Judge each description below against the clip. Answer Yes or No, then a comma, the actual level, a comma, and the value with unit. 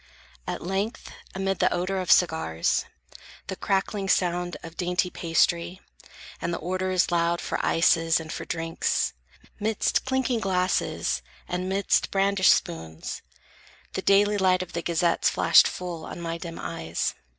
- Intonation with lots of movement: No, narrow, 2.5 semitones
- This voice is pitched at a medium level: Yes, medium, 180 Hz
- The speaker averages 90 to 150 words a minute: Yes, average, 140 wpm